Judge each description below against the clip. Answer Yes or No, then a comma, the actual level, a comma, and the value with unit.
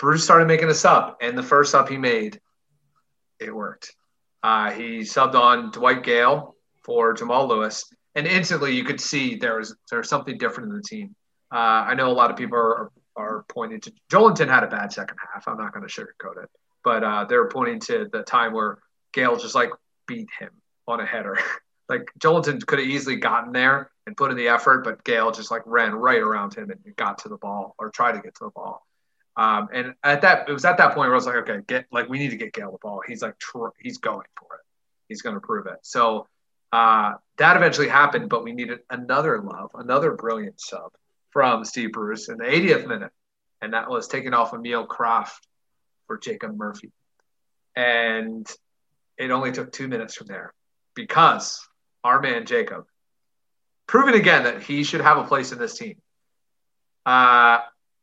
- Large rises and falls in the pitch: Yes, wide, 8.9 semitones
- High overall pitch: No, medium, 140 Hz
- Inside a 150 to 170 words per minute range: No, fast, 205 wpm